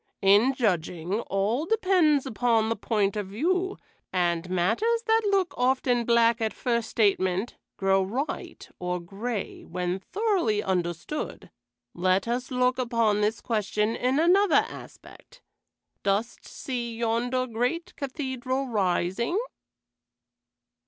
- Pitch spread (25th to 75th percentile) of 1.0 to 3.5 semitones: No, average, 5.2 semitones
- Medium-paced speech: No, slow, 115 wpm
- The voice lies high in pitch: Yes, high, 235 Hz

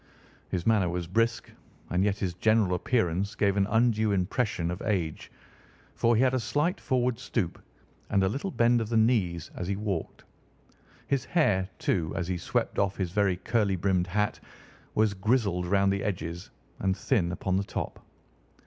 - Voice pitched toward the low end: Yes, low, 100 Hz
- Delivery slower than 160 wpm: No, average, 175 wpm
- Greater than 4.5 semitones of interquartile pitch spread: No, average, 3.9 semitones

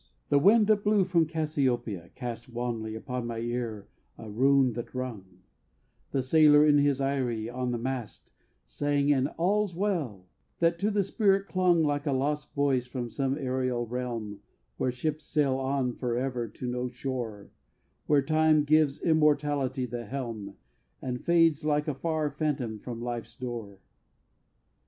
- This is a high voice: No, low, 135 Hz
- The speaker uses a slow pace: No, average, 155 wpm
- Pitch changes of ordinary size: Yes, average, 4.0 semitones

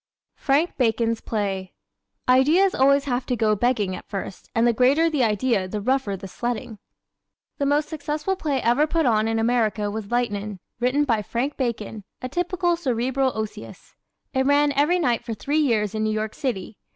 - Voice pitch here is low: No, high, 245 Hz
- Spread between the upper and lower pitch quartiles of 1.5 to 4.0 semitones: No, average, 4.7 semitones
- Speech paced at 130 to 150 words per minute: No, average, 180 wpm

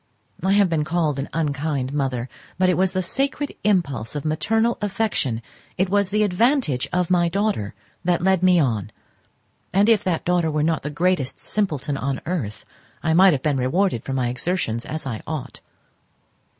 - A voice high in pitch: No, medium, 165 Hz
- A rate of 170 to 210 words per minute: Yes, average, 175 wpm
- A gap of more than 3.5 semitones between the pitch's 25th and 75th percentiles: Yes, wide, 5.5 semitones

